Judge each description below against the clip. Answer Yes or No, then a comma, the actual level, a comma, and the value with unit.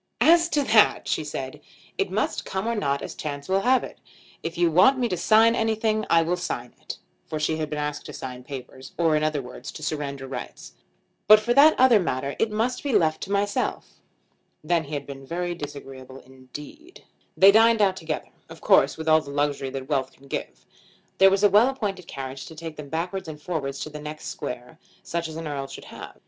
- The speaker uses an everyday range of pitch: No, wide, 6.4 semitones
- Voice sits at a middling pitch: Yes, medium, 160 Hz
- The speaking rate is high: Yes, fast, 215 wpm